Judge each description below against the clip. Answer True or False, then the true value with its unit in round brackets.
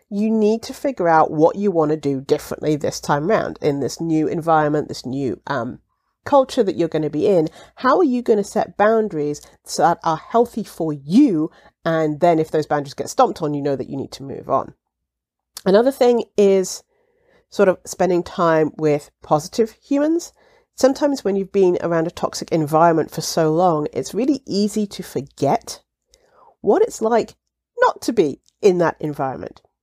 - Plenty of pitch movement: True (7.4 semitones)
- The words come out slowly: False (185 wpm)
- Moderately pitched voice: True (180 Hz)